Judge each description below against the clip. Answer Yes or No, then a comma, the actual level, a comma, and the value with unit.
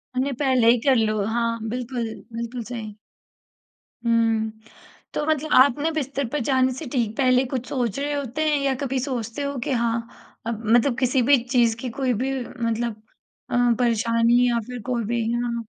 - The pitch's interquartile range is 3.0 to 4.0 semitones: No, narrow, 2.5 semitones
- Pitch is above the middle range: Yes, high, 245 Hz